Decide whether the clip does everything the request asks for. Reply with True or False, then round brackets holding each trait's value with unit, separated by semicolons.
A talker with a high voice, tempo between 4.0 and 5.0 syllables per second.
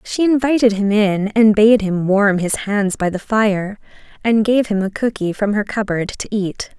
True (210 Hz; 4.4 syllables/s)